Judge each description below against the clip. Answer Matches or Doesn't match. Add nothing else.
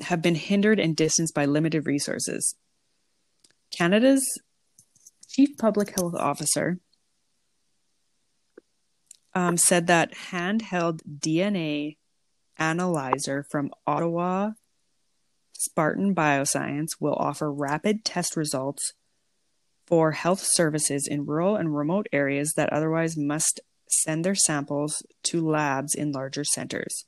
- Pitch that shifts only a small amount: Doesn't match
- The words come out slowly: Matches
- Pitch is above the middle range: Doesn't match